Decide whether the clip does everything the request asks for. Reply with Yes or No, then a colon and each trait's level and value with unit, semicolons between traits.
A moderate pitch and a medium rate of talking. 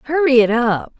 No: very high, 255 Hz; average, 180 wpm